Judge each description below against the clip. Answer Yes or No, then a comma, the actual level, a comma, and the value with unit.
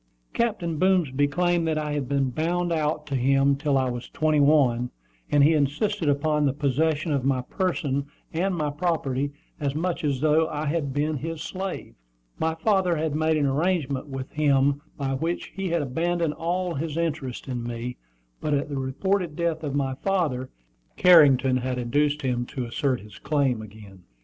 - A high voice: No, medium, 150 Hz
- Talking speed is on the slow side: No, average, 180 wpm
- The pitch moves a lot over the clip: No, average, 3.5 semitones